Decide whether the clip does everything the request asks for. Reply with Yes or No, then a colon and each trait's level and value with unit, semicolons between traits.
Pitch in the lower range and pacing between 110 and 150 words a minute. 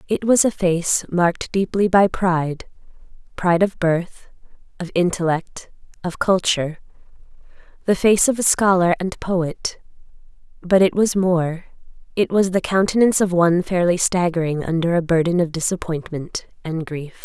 No: medium, 180 Hz; average, 140 wpm